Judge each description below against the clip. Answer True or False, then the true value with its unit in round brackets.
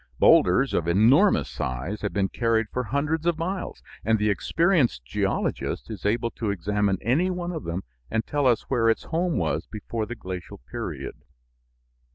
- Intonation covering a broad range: True (7.0 semitones)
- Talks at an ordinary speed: True (170 wpm)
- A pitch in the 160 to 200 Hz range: False (115 Hz)